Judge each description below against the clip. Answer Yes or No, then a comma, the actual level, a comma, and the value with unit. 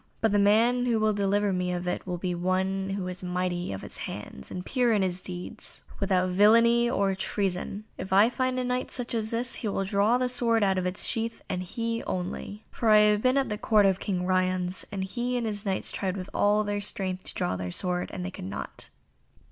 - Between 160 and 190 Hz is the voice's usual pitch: No, high, 200 Hz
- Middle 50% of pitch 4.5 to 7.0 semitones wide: No, average, 3.6 semitones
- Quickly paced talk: Yes, fast, 230 wpm